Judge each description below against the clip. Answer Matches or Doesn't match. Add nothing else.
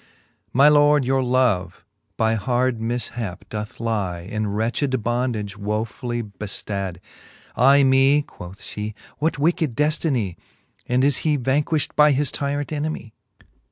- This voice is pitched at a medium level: Doesn't match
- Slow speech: Matches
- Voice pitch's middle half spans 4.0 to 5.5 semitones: Matches